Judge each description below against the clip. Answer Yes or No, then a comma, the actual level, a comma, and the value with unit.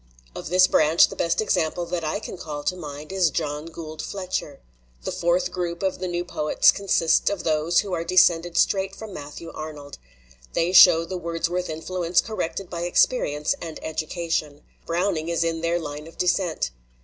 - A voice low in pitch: No, medium, 170 Hz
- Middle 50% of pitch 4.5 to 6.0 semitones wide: No, narrow, 2.4 semitones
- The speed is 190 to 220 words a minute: No, average, 175 wpm